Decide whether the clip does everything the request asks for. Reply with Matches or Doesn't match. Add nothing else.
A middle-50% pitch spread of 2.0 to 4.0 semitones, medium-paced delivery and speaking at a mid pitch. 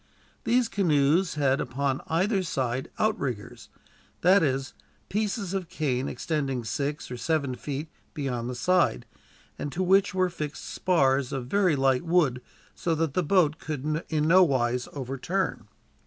Doesn't match